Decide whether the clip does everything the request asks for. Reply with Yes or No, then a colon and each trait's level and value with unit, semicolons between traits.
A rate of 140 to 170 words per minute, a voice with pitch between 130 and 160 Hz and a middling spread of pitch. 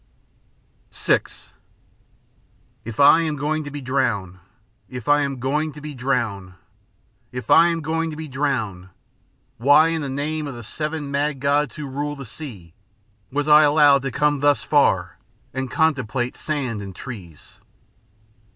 Yes: average, 150 wpm; medium, 140 Hz; average, 3.5 semitones